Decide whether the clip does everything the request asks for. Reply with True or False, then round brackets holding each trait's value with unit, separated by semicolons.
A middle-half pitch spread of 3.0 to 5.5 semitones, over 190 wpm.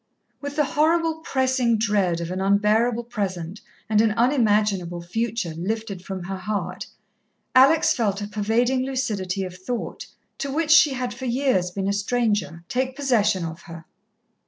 False (5.1 semitones; 155 wpm)